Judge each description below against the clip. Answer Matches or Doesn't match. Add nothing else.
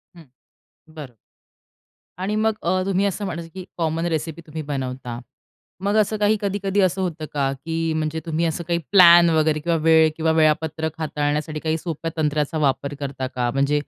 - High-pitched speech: Doesn't match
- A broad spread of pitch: Doesn't match